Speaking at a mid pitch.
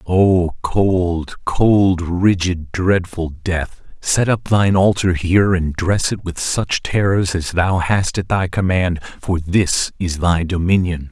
No: very low, 90 Hz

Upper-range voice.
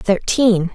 Yes: high, 205 Hz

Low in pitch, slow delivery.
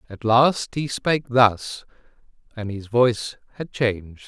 Yes: low, 115 Hz; slow, 125 wpm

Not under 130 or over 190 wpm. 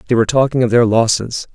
No: fast, 235 wpm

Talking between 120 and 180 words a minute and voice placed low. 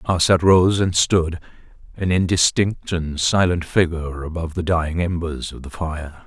Yes: average, 155 wpm; very low, 85 Hz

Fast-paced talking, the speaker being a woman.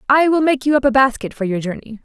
Yes: fast, 295 wpm; female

